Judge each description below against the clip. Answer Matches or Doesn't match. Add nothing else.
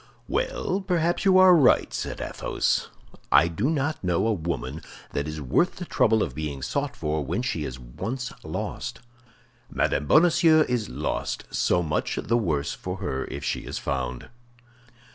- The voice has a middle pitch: Doesn't match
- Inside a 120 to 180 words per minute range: Matches